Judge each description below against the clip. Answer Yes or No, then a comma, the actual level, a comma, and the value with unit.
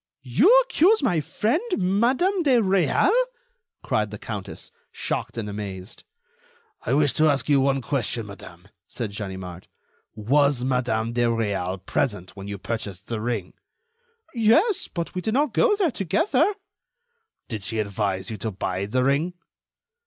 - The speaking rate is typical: Yes, average, 145 wpm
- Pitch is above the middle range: No, low, 120 Hz